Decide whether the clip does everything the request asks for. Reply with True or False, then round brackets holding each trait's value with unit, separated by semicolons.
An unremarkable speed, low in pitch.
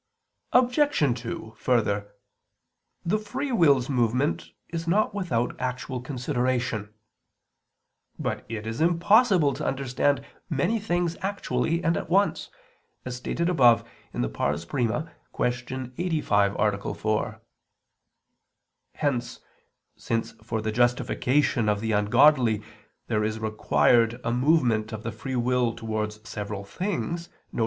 False (115 wpm; 125 Hz)